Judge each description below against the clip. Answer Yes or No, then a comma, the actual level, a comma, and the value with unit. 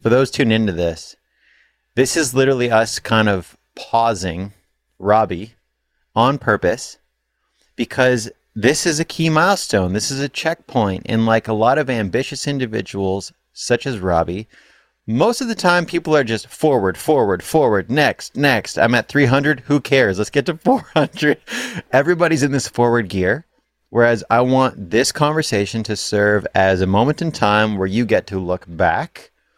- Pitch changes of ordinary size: No, wide, 6.0 semitones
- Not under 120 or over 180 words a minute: Yes, average, 160 wpm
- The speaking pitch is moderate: No, low, 120 Hz